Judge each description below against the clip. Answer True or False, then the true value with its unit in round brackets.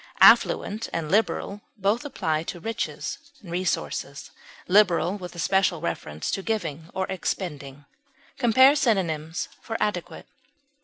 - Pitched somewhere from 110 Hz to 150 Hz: False (185 Hz)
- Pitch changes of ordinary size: True (4.4 semitones)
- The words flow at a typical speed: False (110 wpm)